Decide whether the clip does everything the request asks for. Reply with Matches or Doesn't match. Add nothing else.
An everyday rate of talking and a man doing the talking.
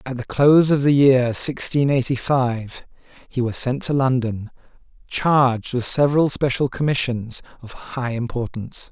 Matches